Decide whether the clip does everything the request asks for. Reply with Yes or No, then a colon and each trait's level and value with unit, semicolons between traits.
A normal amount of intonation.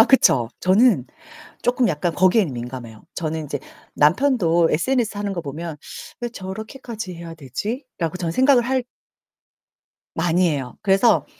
No: wide, 6.9 semitones